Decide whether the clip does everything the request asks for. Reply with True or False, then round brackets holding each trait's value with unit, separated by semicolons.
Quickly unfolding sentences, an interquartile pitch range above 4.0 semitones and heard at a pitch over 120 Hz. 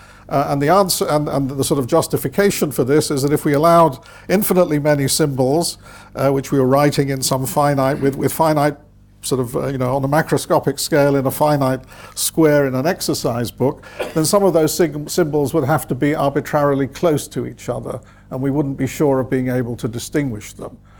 False (210 wpm; 2.8 semitones; 140 Hz)